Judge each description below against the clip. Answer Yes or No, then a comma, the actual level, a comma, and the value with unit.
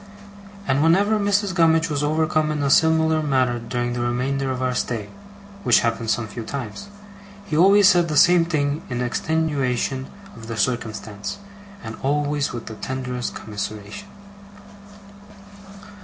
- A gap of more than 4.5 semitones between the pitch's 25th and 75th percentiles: Yes, average, 5.0 semitones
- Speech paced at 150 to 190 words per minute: No, average, 140 wpm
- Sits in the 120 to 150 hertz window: Yes, medium, 140 Hz